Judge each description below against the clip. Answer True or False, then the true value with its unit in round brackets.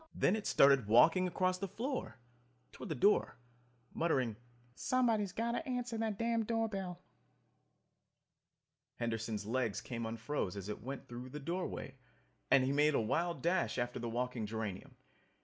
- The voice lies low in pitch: False (145 Hz)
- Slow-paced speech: False (150 wpm)